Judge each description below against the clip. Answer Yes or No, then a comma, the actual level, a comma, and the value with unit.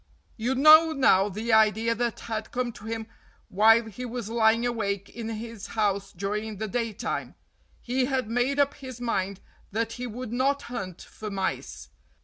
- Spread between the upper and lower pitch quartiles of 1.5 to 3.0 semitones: Yes, narrow, 2.6 semitones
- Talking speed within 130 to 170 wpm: Yes, average, 165 wpm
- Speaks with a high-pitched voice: Yes, high, 225 Hz